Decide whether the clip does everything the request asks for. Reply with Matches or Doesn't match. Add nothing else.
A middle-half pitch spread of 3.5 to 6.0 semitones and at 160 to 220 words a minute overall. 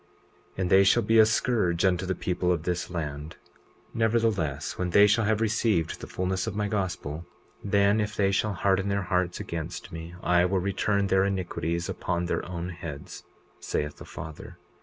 Doesn't match